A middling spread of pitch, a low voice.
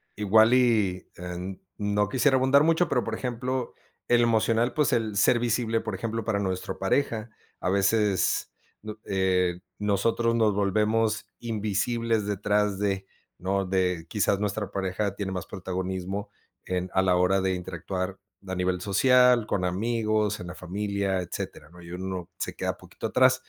Yes: average, 3.3 semitones; low, 105 Hz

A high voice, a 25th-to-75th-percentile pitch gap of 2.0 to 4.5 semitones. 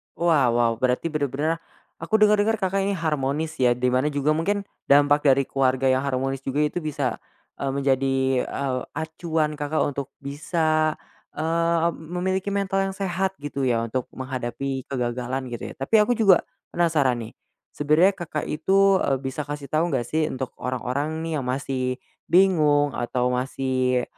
No: medium, 145 Hz; average, 4.0 semitones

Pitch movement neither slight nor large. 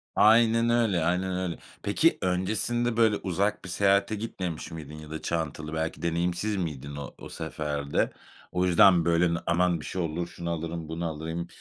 Yes: average, 3.3 semitones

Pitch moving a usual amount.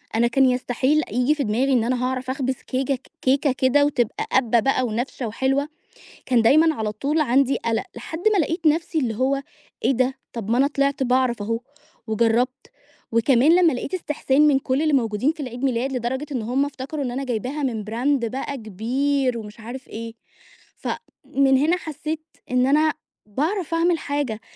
Yes: average, 3.3 semitones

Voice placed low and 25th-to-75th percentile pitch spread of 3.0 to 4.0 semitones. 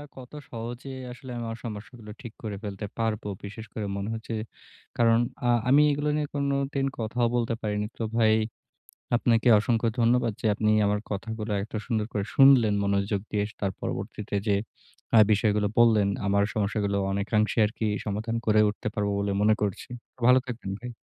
No: low, 110 Hz; narrow, 2.4 semitones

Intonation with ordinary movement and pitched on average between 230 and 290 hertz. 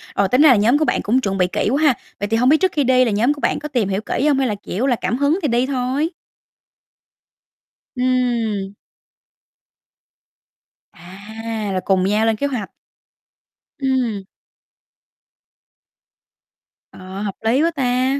Yes: average, 4.6 semitones; high, 245 Hz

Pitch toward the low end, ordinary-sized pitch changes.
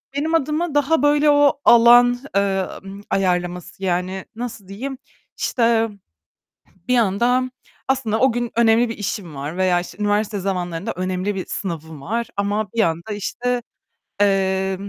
No: high, 210 Hz; average, 4.6 semitones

